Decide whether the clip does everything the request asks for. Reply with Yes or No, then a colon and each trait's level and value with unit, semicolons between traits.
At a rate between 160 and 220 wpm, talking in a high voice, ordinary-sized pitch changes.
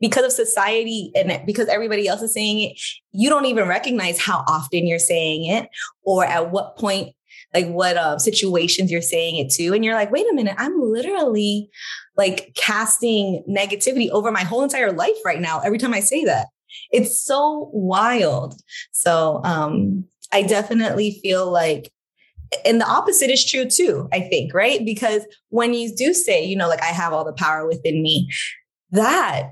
Yes: average, 180 wpm; high, 205 Hz; average, 4.9 semitones